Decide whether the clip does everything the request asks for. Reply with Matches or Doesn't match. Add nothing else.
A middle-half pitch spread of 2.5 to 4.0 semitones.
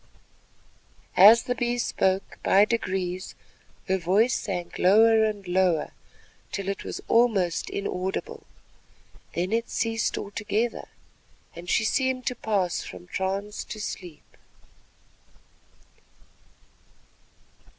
Matches